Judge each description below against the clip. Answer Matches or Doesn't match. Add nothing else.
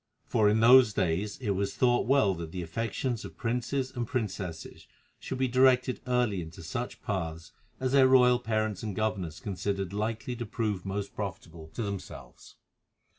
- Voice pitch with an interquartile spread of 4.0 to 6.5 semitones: Matches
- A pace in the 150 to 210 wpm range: Matches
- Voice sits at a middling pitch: Doesn't match